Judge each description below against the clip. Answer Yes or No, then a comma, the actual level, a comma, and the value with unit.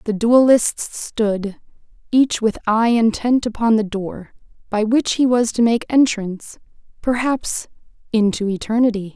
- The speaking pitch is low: No, high, 225 Hz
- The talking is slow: Yes, slow, 130 wpm